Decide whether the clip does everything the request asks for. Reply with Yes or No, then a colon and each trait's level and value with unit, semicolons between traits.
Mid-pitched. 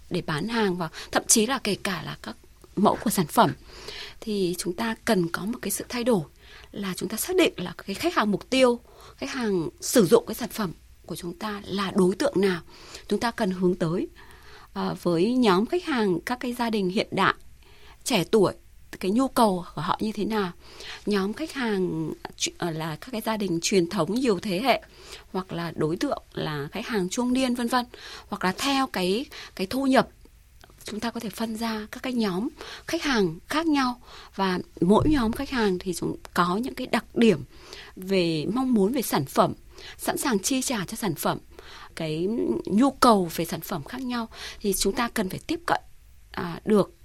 No: high, 210 Hz